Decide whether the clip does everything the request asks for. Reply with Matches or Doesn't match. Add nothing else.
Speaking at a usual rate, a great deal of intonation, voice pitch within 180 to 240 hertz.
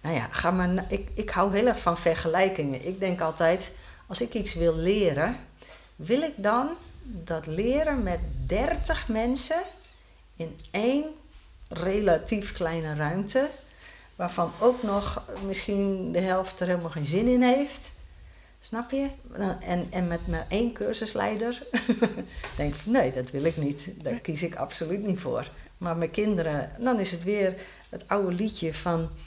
Matches